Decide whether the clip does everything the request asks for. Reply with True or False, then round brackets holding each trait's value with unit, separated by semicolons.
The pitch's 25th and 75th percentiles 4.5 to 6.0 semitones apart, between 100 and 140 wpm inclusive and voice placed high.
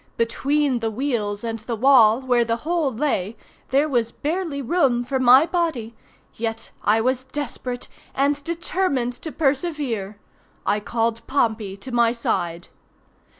False (4.0 semitones; 135 wpm; 245 Hz)